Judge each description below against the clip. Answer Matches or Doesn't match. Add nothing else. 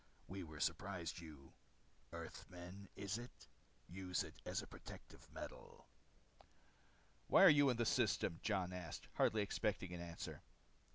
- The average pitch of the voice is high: Doesn't match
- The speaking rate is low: Matches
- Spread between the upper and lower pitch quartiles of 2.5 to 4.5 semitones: Matches